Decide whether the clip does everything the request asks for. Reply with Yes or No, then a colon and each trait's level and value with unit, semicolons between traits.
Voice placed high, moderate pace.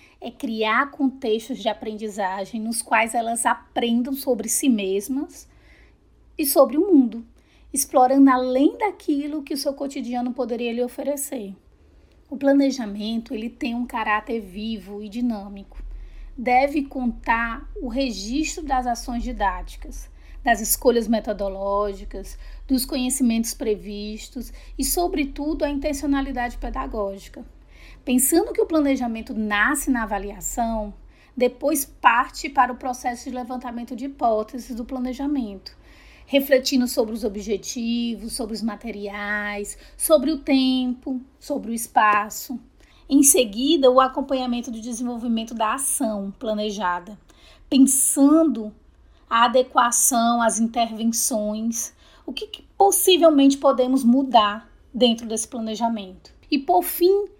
No: high, 245 Hz; slow, 115 wpm